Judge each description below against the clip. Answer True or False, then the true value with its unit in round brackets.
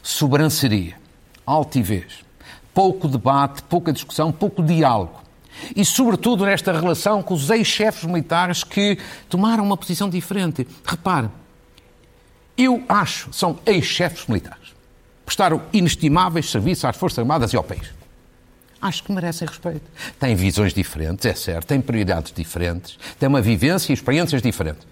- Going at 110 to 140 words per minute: True (130 wpm)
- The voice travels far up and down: True (8.3 semitones)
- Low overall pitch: False (150 Hz)